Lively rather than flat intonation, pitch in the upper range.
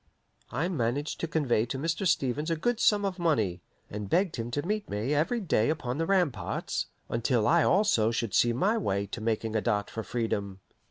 No: wide, 7.3 semitones; low, 130 Hz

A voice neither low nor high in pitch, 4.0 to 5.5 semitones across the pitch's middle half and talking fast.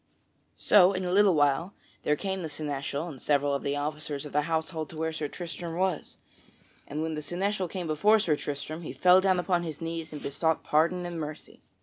No: medium, 160 Hz; average, 3.3 semitones; fast, 210 wpm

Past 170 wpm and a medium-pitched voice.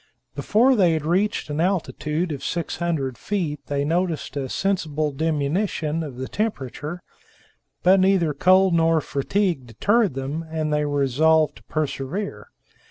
No: average, 140 wpm; medium, 160 Hz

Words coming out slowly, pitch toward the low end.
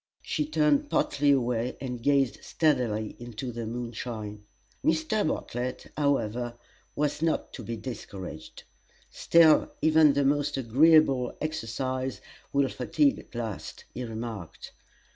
Yes: slow, 120 wpm; low, 130 Hz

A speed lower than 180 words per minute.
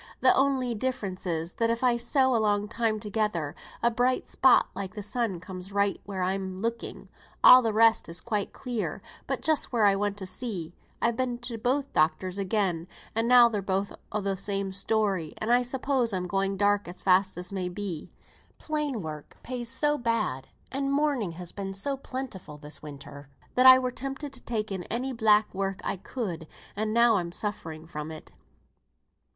No: average, 185 wpm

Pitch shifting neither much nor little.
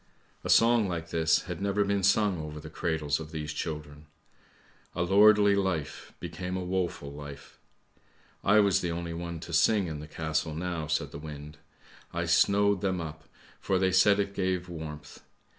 Yes: average, 3.9 semitones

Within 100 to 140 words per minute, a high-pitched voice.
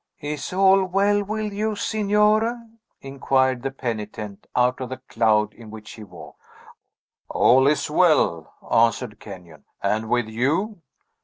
No: slow, 135 wpm; low, 130 Hz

